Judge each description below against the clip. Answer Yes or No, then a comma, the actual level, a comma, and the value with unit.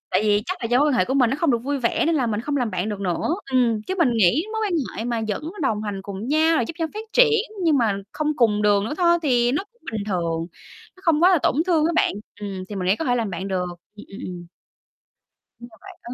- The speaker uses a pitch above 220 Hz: Yes, high, 240 Hz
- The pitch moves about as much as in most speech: No, wide, 7.0 semitones